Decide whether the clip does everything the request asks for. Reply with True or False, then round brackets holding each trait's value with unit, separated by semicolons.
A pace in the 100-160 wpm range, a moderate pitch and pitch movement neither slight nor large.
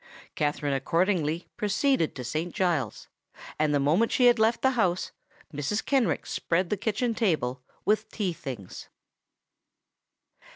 False (135 wpm; 175 Hz; 6.9 semitones)